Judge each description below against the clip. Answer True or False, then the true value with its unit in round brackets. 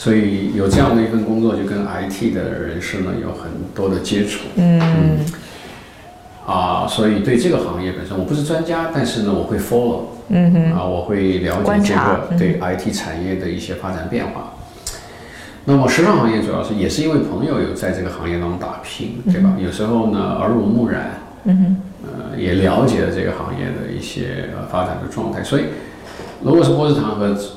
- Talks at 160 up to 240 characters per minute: False (295 characters per minute)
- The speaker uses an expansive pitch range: True (8.3 semitones)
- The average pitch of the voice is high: False (105 Hz)